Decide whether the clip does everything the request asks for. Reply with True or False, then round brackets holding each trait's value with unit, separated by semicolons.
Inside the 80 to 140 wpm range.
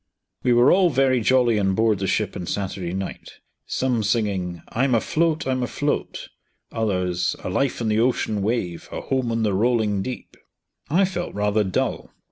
False (170 wpm)